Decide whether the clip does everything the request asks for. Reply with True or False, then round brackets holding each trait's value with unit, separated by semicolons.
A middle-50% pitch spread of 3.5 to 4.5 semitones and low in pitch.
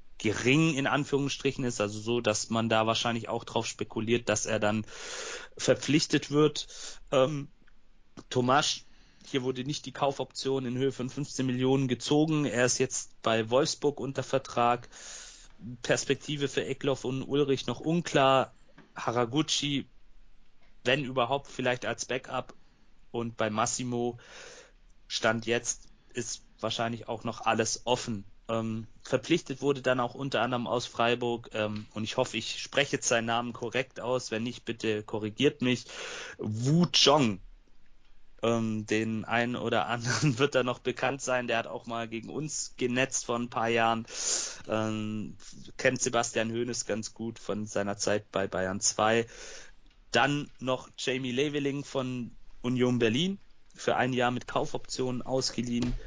False (3.0 semitones; 120 Hz)